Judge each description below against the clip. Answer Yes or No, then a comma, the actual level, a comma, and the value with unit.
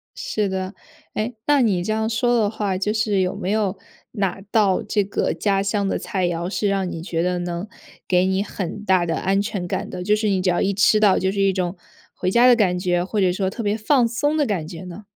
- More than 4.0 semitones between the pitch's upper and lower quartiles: No, average, 2.8 semitones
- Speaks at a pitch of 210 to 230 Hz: No, high, 195 Hz